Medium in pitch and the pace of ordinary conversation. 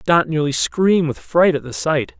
No: medium, 150 Hz; fast, 220 wpm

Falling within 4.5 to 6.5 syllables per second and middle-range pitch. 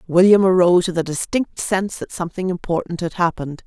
Yes: 6.3 syllables/s; medium, 175 Hz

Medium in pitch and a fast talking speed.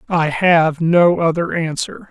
No: medium, 165 Hz; average, 145 wpm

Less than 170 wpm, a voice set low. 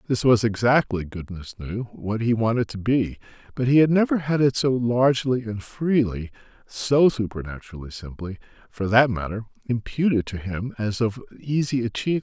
Yes: average, 150 wpm; low, 115 Hz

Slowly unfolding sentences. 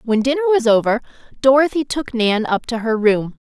No: average, 190 wpm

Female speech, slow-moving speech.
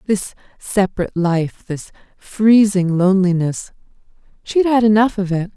Yes: female; slow, 130 wpm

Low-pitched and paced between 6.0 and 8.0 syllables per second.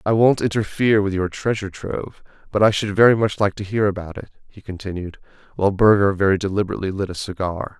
Yes: low, 100 Hz; 6.6 syllables/s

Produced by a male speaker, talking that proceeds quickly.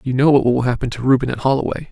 Yes: male; fast, 280 wpm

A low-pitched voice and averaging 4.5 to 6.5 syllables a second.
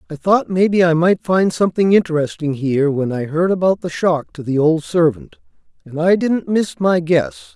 No: medium, 170 Hz; 5.1 syllables/s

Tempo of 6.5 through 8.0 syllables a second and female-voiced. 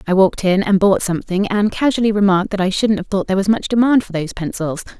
Yes: 6.8 syllables/s; female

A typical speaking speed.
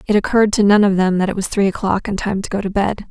No: fast, 330 wpm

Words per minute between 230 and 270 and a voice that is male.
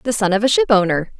No: fast, 250 wpm; female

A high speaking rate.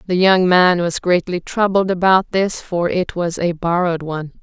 No: average, 190 wpm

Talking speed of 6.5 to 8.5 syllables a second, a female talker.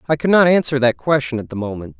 No: 6.6 syllables/s; male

